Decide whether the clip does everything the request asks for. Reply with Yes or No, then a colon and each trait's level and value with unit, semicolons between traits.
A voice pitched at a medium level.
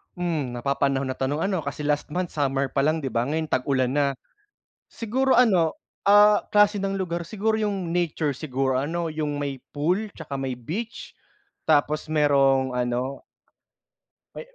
Yes: medium, 150 Hz